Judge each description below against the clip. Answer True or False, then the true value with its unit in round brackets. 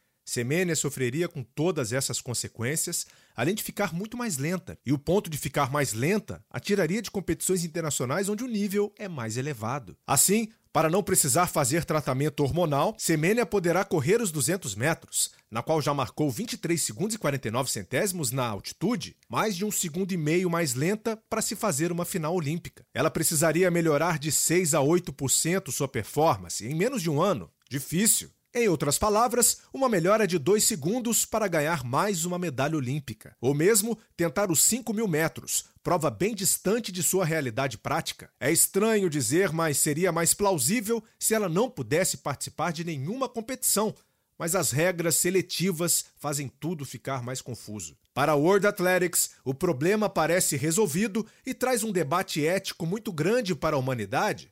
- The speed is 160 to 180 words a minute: True (170 wpm)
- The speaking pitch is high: False (170 Hz)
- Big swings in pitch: True (5.7 semitones)